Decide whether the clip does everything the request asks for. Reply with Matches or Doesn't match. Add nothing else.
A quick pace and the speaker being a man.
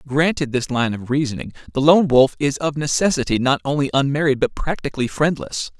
Doesn't match